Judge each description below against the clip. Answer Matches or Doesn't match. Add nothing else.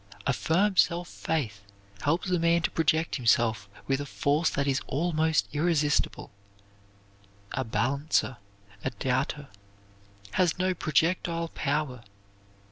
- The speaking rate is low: Matches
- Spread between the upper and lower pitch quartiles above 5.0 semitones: Doesn't match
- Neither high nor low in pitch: Matches